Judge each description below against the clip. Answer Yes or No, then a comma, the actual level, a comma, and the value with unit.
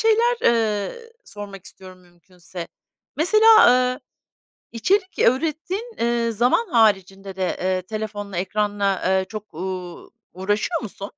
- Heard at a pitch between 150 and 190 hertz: No, high, 210 Hz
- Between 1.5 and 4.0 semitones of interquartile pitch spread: No, average, 5.0 semitones